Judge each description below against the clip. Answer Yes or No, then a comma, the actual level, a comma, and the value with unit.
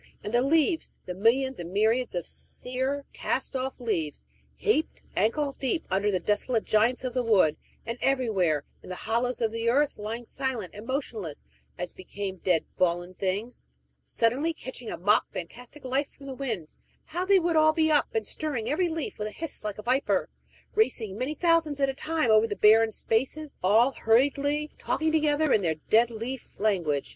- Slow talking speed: No, average, 185 wpm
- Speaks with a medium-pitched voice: No, high, 240 Hz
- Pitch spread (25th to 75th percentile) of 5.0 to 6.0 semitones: Yes, wide, 5.4 semitones